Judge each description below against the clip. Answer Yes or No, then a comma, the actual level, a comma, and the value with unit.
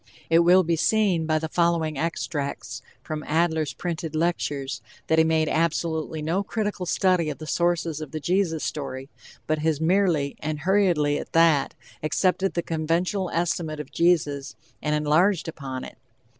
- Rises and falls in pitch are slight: Yes, narrow, 2.3 semitones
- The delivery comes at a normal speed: Yes, average, 160 wpm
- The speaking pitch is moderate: Yes, medium, 160 Hz